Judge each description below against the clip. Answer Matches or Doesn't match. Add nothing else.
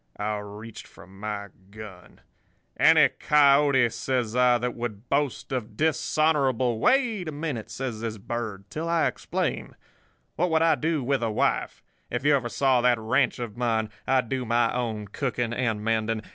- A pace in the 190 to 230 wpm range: Doesn't match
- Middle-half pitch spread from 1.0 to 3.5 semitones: Doesn't match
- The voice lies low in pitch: Matches